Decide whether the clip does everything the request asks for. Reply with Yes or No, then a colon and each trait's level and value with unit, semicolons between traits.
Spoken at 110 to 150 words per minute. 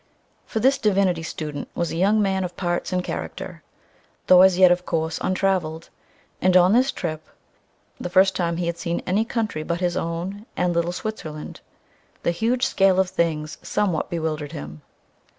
No: average, 170 wpm